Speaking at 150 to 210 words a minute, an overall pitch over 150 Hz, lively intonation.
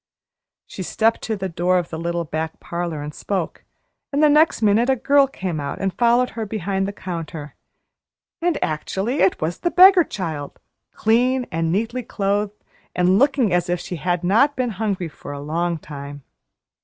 Yes: average, 180 wpm; high, 190 Hz; wide, 5.9 semitones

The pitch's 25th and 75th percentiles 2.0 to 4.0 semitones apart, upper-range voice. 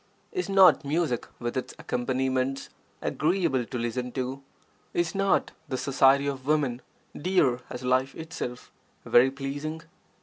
No: average, 3.6 semitones; low, 135 Hz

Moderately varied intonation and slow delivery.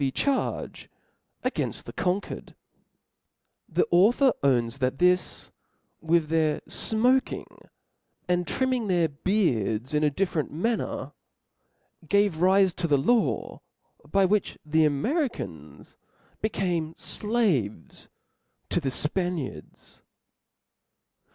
No: wide, 6.1 semitones; slow, 85 wpm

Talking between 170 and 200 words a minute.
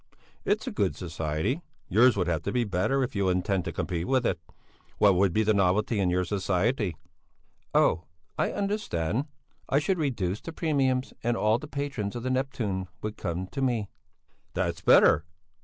Yes: average, 175 wpm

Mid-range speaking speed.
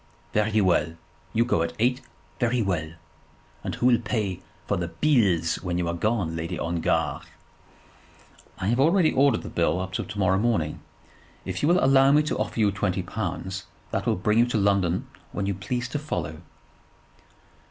Yes: average, 175 wpm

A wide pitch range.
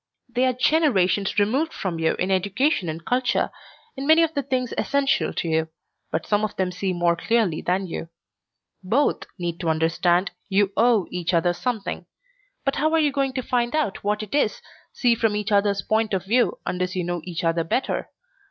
Yes: wide, 6.1 semitones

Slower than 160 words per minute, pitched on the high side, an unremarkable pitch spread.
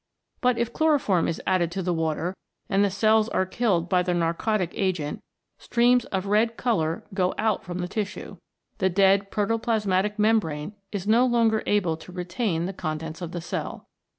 No: average, 175 wpm; high, 195 Hz; average, 3.9 semitones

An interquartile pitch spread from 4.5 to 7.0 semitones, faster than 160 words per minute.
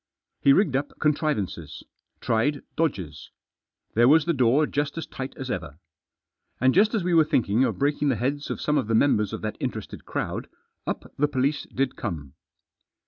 Yes: average, 4.9 semitones; average, 180 wpm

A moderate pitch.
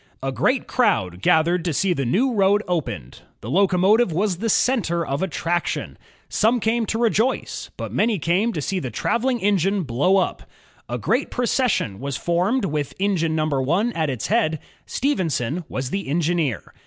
Yes: medium, 180 Hz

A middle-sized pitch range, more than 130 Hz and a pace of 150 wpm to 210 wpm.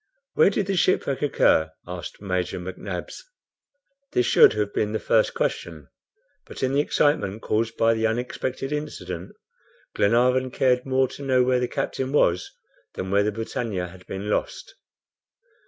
No: average, 4.9 semitones; low, 115 Hz; average, 155 wpm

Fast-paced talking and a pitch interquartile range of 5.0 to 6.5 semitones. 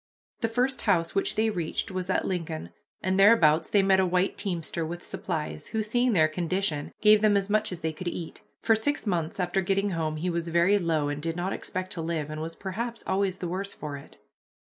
No: fast, 220 wpm; average, 3.4 semitones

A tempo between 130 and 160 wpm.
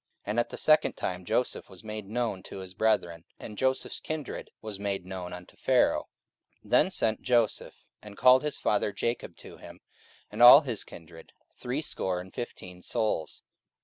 No: average, 175 wpm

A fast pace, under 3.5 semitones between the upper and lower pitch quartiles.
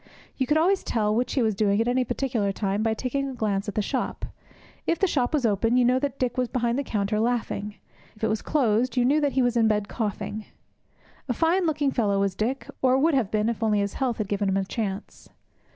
No: fast, 245 wpm; average, 3.9 semitones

